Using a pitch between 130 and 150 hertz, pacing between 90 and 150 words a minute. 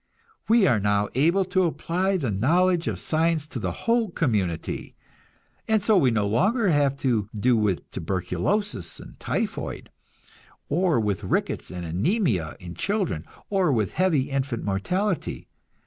Yes: medium, 140 Hz; average, 145 wpm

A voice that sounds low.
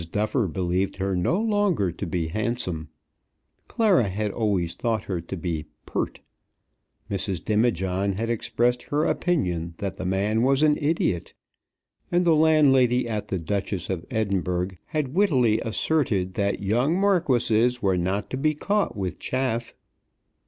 Yes: low, 110 Hz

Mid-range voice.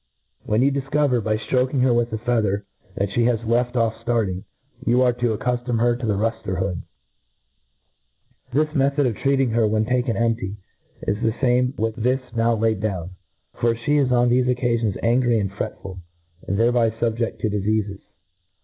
No: low, 115 Hz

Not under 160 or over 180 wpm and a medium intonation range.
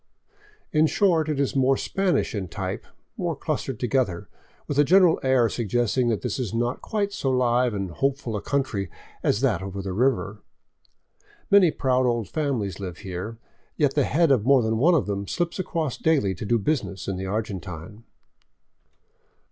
No: average, 170 wpm; wide, 5.7 semitones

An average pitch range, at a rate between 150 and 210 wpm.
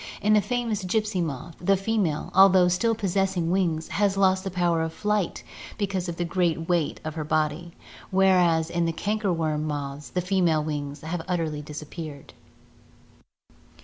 Yes: average, 3.4 semitones; average, 160 wpm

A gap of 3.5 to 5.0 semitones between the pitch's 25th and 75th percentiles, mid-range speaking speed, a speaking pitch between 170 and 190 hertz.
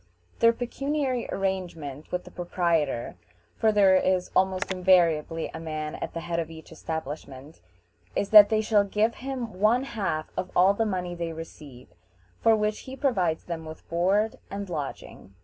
Yes: average, 4.7 semitones; average, 165 wpm; medium, 185 Hz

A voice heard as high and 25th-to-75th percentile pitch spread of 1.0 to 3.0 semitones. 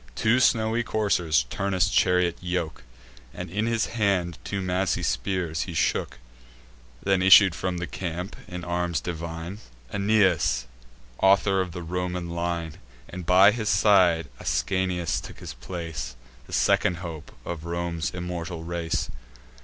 No: very low, 90 Hz; narrow, 2.4 semitones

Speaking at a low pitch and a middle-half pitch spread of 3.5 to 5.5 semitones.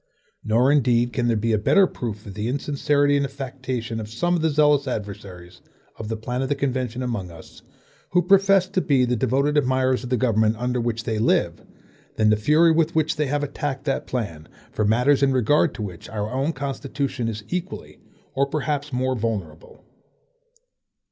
Yes: low, 130 Hz; average, 4.4 semitones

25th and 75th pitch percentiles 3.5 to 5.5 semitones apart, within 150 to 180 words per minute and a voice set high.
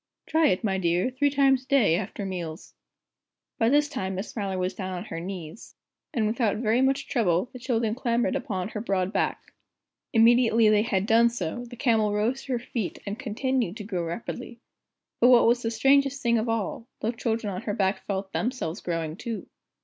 No: average, 4.2 semitones; average, 195 wpm; high, 225 Hz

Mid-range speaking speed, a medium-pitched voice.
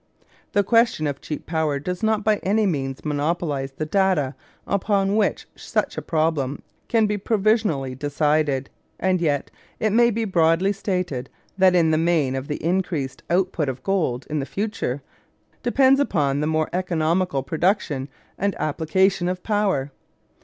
Yes: average, 150 wpm; medium, 170 Hz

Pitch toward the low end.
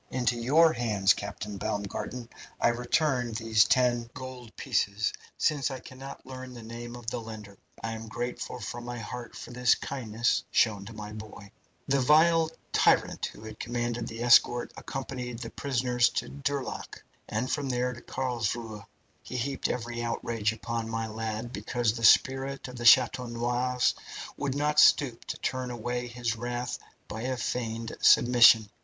Yes: low, 120 Hz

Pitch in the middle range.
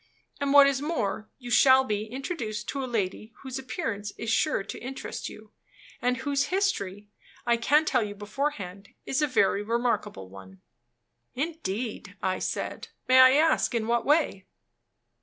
No: high, 240 Hz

